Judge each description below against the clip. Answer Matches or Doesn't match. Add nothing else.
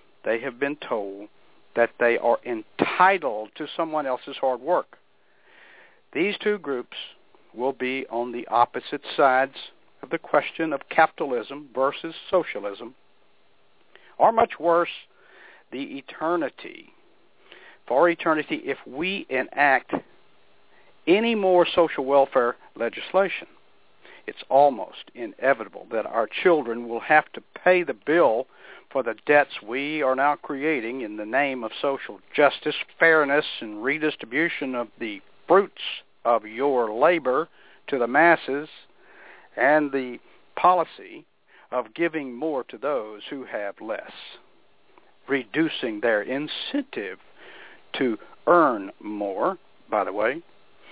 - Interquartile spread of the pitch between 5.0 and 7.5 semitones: Matches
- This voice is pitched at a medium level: Matches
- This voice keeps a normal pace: Doesn't match